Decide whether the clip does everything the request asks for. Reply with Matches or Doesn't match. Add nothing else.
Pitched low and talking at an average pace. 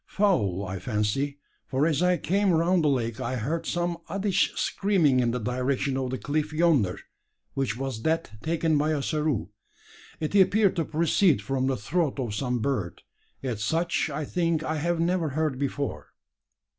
Doesn't match